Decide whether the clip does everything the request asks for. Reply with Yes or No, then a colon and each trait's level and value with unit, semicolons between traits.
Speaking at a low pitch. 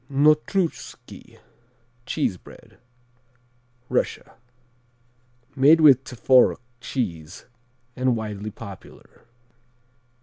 Yes: low, 125 Hz